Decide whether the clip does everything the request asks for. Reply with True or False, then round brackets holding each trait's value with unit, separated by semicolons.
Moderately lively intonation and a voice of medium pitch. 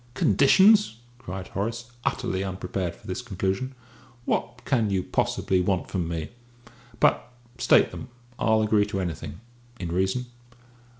False (4.2 semitones; 95 Hz)